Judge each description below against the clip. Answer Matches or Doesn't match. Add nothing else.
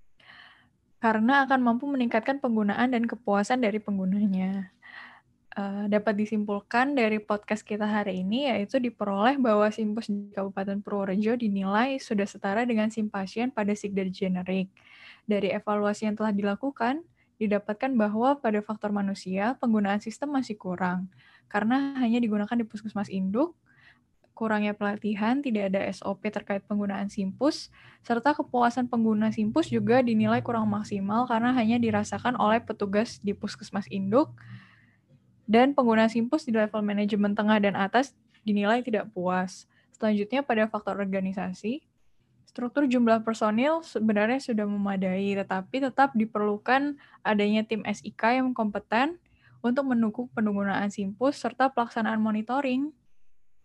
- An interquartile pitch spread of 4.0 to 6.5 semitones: Doesn't match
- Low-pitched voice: Doesn't match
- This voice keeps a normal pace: Matches